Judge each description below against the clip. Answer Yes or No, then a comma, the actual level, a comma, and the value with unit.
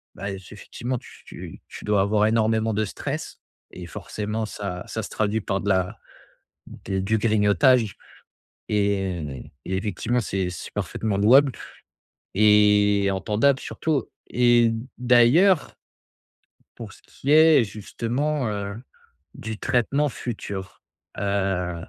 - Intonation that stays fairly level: No, average, 3.3 semitones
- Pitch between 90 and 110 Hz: Yes, low, 105 Hz